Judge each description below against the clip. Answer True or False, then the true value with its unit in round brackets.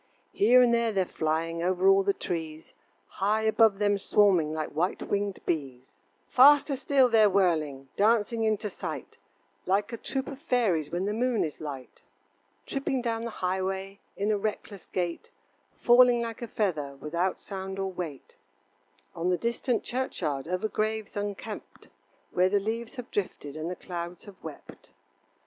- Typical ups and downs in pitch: True (4.7 semitones)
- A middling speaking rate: True (160 wpm)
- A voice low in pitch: False (200 Hz)